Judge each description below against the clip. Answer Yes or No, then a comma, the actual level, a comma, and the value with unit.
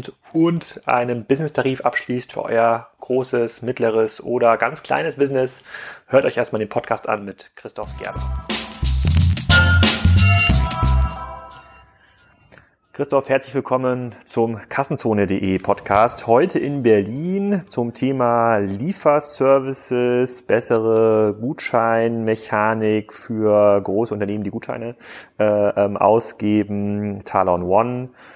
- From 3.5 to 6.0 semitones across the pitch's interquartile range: Yes, average, 3.8 semitones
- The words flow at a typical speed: No, slow, 90 wpm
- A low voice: Yes, low, 115 Hz